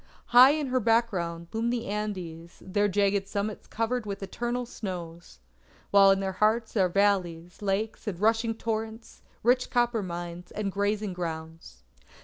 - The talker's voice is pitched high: Yes, high, 205 Hz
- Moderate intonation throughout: Yes, average, 3.9 semitones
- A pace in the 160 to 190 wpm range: No, average, 145 wpm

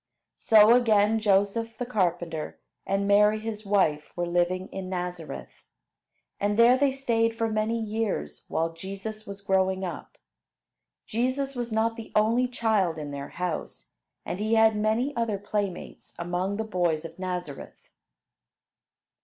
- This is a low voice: No, high, 205 Hz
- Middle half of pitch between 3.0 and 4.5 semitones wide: Yes, average, 3.8 semitones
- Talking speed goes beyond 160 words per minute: No, average, 140 wpm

